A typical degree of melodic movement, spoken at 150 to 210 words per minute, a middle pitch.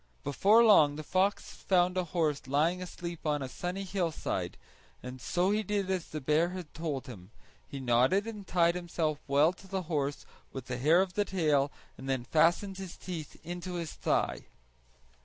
Yes: average, 4.3 semitones; average, 180 wpm; medium, 170 Hz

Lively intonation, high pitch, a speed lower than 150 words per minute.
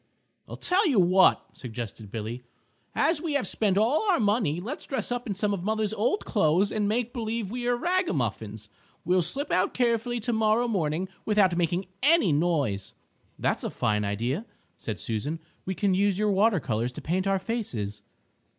No: wide, 7.5 semitones; high, 195 Hz; average, 180 wpm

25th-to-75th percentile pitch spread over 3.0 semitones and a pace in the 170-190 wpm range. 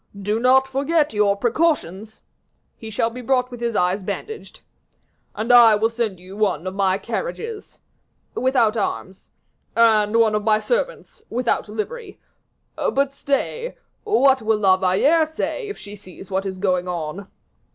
No: average, 5.1 semitones; average, 150 wpm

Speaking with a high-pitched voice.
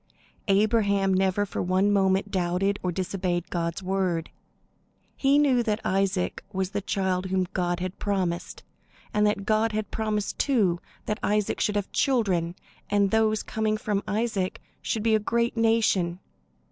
Yes: high, 200 Hz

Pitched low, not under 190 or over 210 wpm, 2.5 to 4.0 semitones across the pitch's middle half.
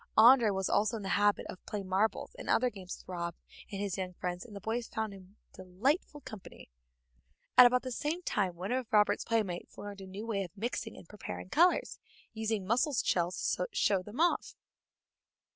No: high, 205 Hz; average, 195 wpm; average, 3.7 semitones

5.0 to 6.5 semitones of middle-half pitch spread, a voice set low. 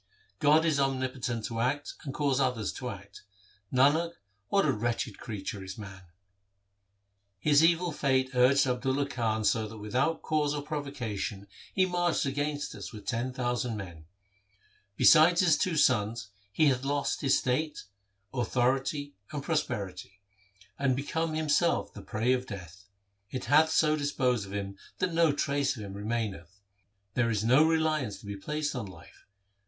Yes: wide, 5.5 semitones; low, 130 Hz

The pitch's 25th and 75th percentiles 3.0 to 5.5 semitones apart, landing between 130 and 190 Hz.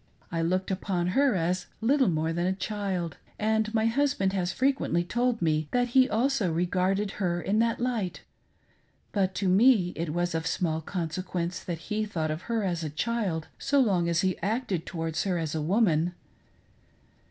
Yes: average, 4.4 semitones; medium, 185 Hz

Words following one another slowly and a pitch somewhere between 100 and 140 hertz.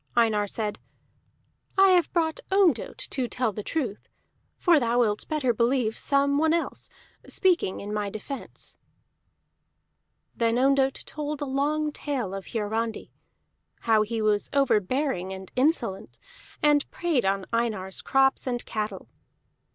No: slow, 130 wpm; high, 245 Hz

